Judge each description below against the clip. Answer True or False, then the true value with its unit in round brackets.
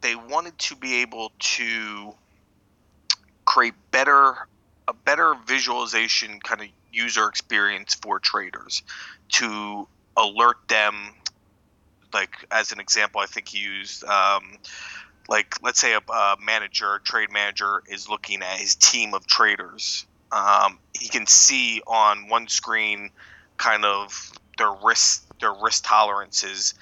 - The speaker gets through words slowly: True (130 wpm)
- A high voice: False (105 Hz)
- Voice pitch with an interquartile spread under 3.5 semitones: True (3.0 semitones)